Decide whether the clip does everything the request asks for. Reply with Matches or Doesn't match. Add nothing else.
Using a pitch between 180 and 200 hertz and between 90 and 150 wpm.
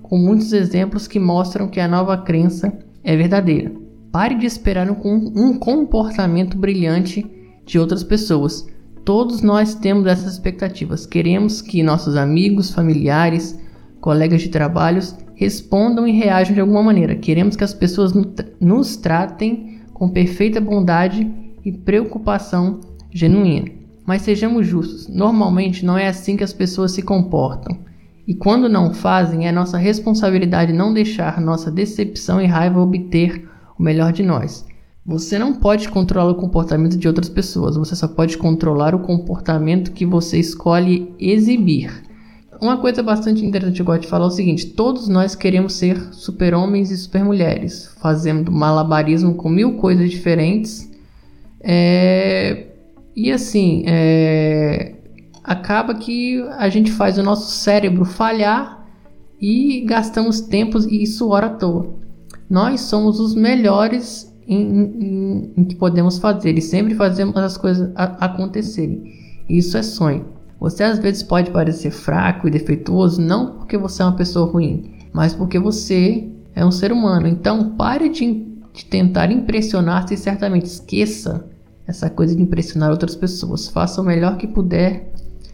Matches